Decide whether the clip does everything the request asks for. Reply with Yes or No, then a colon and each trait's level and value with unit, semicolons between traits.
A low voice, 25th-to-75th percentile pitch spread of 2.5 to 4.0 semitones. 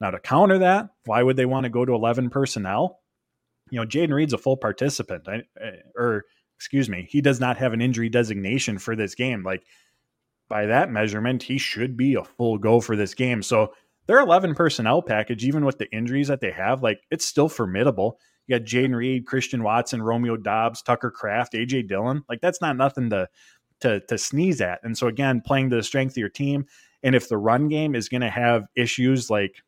Yes: low, 125 Hz; average, 2.9 semitones